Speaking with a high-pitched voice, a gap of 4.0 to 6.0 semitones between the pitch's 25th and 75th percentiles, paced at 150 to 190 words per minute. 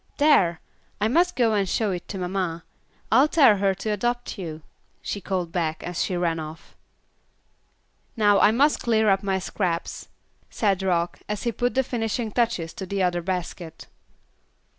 Yes: high, 195 Hz; average, 4.3 semitones; average, 165 wpm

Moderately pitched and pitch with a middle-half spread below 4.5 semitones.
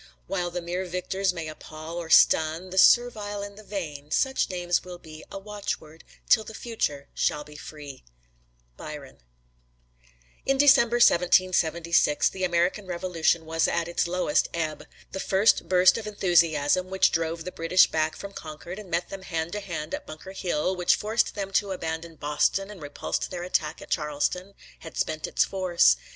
Yes: medium, 175 Hz; average, 3.3 semitones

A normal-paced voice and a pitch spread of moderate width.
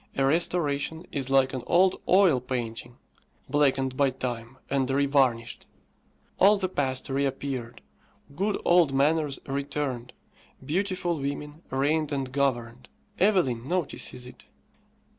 No: slow, 115 wpm; average, 3.6 semitones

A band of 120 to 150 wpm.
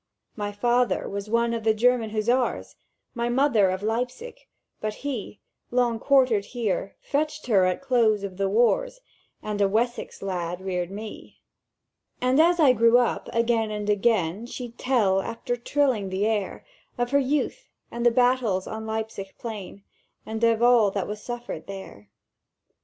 No: average, 160 wpm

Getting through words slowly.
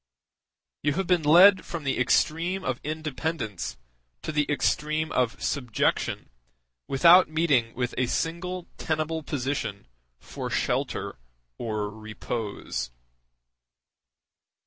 Yes: slow, 100 wpm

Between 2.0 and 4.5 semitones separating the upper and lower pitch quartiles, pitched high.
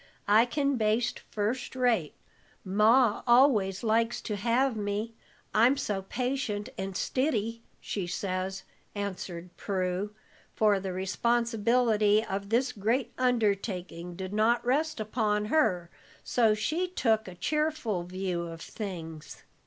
Yes: average, 3.8 semitones; high, 215 Hz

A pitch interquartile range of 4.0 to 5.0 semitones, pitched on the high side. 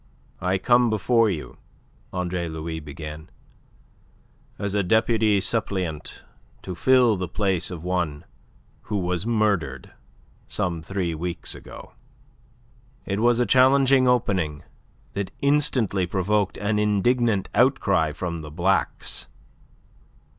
No: average, 4.6 semitones; very low, 95 Hz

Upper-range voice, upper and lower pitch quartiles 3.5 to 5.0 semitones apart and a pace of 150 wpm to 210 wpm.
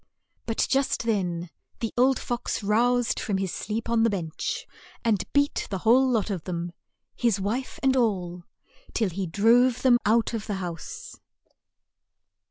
Yes: high, 225 Hz; average, 4.2 semitones; average, 155 wpm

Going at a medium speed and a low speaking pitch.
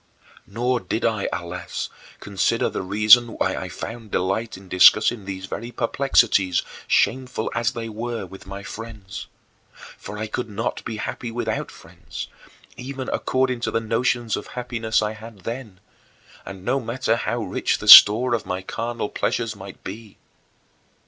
Yes: average, 155 wpm; low, 110 Hz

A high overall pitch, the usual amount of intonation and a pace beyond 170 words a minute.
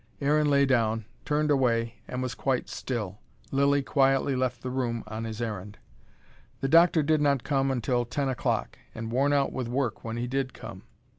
No: low, 130 Hz; average, 3.1 semitones; average, 180 wpm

